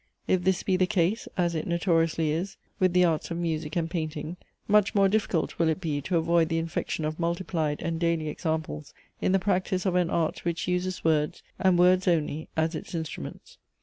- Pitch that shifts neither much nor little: No, narrow, 2.3 semitones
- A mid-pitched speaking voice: Yes, medium, 170 Hz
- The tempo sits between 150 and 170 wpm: No, average, 200 wpm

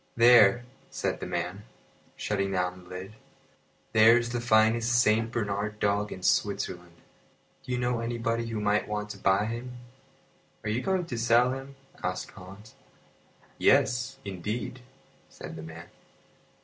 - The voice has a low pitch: Yes, low, 110 Hz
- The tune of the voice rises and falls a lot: No, average, 3.2 semitones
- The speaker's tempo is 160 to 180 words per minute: No, average, 145 wpm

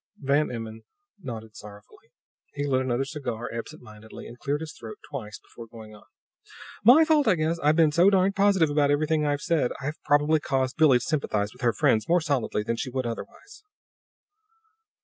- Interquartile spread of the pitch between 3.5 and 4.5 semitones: No, average, 5.3 semitones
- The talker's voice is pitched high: No, medium, 140 Hz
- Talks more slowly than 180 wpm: No, average, 185 wpm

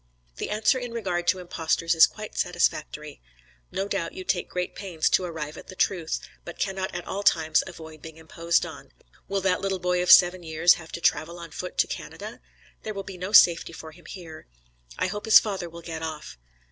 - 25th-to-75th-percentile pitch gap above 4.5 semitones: No, average, 2.8 semitones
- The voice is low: No, medium, 175 Hz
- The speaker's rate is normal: No, fast, 210 wpm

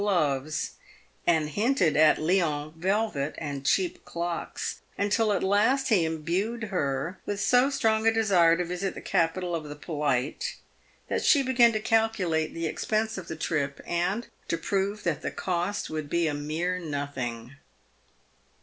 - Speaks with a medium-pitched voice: Yes, medium, 175 Hz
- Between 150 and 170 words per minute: Yes, average, 155 wpm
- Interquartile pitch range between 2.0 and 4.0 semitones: No, average, 5.2 semitones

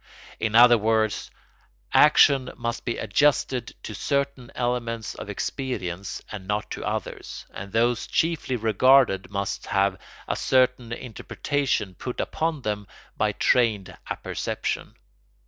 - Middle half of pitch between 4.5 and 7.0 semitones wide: No, average, 3.6 semitones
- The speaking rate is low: Yes, slow, 120 wpm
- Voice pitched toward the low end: Yes, low, 115 Hz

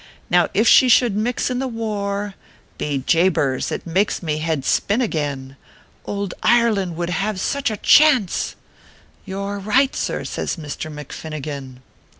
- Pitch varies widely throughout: Yes, wide, 6.1 semitones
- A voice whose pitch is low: No, high, 195 Hz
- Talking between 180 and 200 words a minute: No, average, 160 wpm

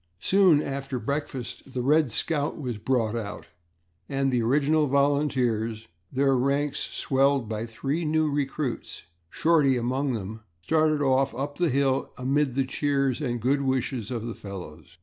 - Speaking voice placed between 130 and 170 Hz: Yes, low, 135 Hz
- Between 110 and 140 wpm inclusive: No, average, 150 wpm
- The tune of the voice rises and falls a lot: No, average, 3.2 semitones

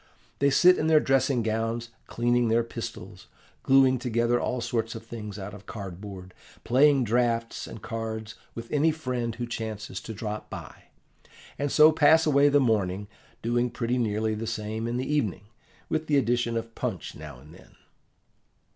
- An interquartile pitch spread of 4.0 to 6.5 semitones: No, average, 3.0 semitones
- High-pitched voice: No, low, 115 Hz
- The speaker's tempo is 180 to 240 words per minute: No, average, 165 wpm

